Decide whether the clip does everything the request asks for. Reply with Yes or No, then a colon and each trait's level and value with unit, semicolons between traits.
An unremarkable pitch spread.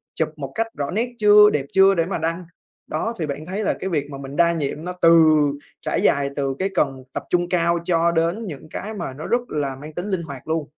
Yes: average, 4.4 semitones